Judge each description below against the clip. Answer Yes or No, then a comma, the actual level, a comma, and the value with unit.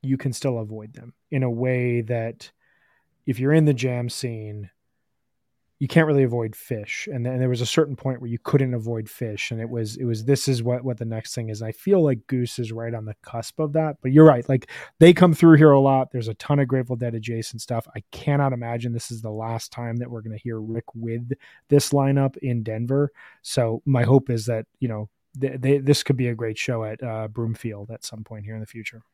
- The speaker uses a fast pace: Yes, fast, 250 wpm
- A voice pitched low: Yes, low, 120 Hz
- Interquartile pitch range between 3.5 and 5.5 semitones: No, average, 3.0 semitones